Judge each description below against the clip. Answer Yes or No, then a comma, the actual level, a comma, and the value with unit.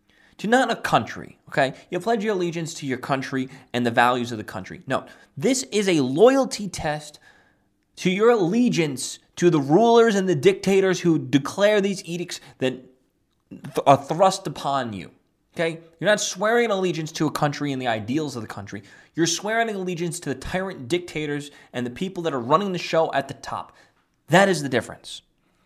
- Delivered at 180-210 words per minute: Yes, average, 185 wpm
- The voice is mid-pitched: Yes, medium, 165 Hz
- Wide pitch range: Yes, wide, 6.1 semitones